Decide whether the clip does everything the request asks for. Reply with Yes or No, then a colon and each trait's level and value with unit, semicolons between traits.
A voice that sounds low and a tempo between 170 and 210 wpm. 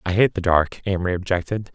Yes: very low, 95 Hz; fast, 205 wpm